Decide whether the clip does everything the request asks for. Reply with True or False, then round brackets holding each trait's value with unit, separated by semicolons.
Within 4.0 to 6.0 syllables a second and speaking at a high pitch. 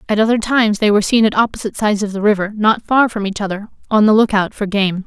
False (6.8 syllables/s; 210 Hz)